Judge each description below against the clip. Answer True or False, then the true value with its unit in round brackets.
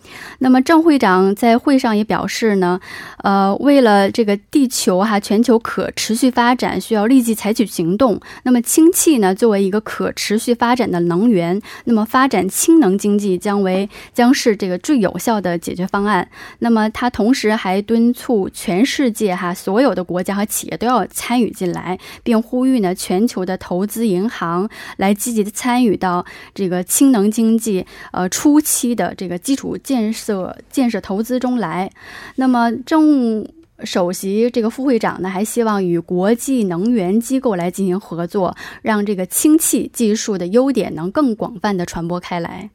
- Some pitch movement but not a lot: True (4.6 semitones)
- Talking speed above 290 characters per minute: False (265 characters per minute)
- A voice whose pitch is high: True (215 Hz)